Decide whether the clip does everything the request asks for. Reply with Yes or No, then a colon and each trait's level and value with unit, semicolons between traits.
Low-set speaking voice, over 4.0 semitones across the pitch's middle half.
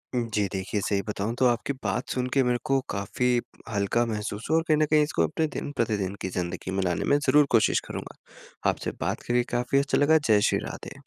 Yes: low, 120 Hz; average, 5.2 semitones